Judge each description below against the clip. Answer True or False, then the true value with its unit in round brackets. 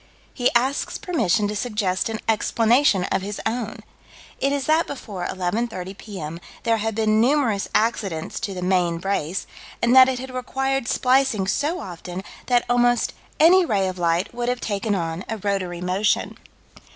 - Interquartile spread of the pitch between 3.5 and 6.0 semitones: True (4.8 semitones)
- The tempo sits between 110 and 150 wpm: False (165 wpm)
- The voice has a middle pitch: False (220 Hz)